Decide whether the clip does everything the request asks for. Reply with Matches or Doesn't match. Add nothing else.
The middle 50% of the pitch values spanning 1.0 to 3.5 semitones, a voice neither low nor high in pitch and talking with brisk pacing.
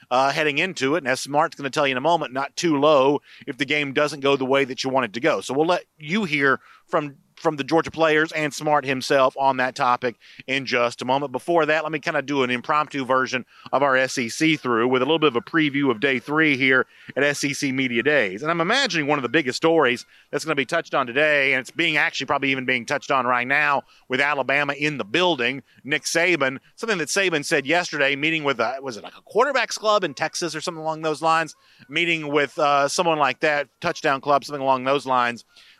Matches